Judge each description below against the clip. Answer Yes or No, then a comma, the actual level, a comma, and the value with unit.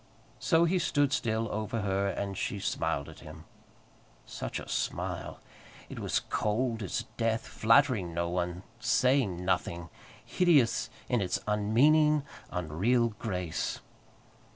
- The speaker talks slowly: Yes, slow, 125 wpm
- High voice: No, low, 110 Hz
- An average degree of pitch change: No, wide, 5.7 semitones